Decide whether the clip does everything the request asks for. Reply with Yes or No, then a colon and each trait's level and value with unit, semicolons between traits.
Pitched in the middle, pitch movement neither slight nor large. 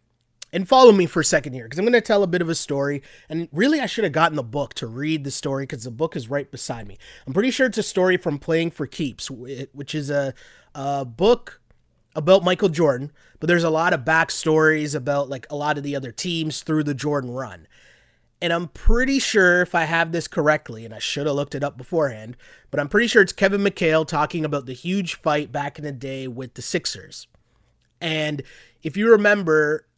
Yes: medium, 155 Hz; average, 3.6 semitones